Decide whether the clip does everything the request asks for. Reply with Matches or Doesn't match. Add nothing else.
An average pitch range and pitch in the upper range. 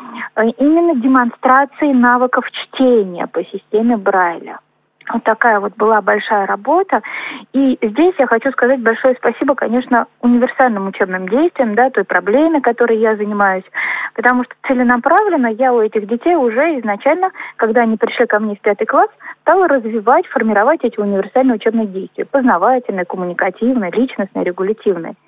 Matches